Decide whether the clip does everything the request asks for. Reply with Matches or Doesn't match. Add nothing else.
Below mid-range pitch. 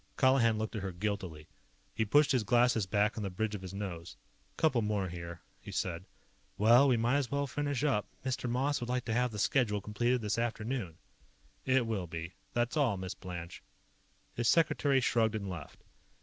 Matches